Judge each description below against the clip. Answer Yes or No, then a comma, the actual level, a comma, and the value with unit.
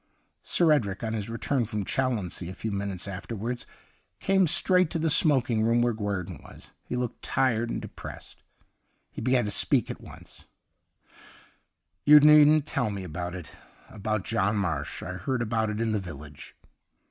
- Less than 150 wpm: No, average, 175 wpm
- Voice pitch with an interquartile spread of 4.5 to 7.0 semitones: Yes, average, 5.2 semitones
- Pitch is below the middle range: Yes, low, 110 Hz